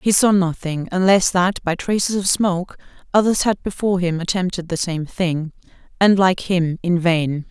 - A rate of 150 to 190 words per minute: Yes, average, 175 wpm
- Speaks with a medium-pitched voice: Yes, medium, 180 Hz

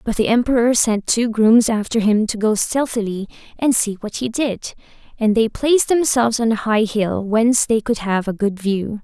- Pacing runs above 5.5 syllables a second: No, 5.0 syllables/s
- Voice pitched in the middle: No, high, 225 Hz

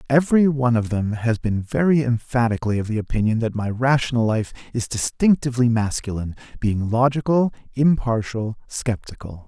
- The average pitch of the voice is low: Yes, low, 120 Hz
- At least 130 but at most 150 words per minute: Yes, average, 140 wpm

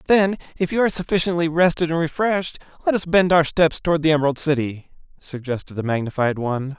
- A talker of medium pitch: Yes, medium, 160 Hz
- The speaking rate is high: No, average, 185 wpm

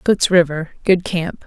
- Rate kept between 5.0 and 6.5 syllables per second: No, 4.0 syllables/s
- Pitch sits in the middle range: Yes, medium, 175 Hz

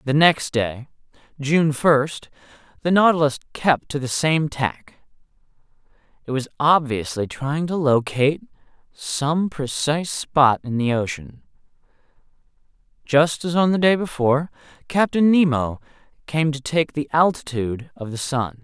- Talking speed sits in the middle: No, slow, 130 wpm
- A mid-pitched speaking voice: Yes, medium, 145 Hz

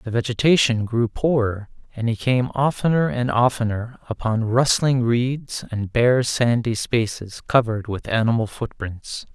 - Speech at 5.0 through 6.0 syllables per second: No, 4.3 syllables/s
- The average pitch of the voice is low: Yes, low, 120 Hz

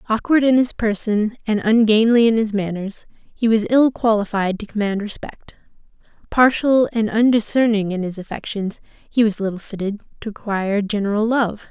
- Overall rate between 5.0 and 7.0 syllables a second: Yes, 5.1 syllables/s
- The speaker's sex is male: No, female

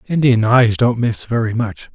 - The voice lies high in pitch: No, low, 115 Hz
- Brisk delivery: No, average, 185 wpm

